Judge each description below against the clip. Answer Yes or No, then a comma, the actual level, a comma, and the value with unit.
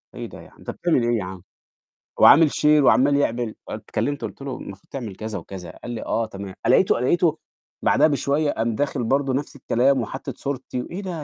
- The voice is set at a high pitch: No, low, 130 Hz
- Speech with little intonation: No, average, 4.3 semitones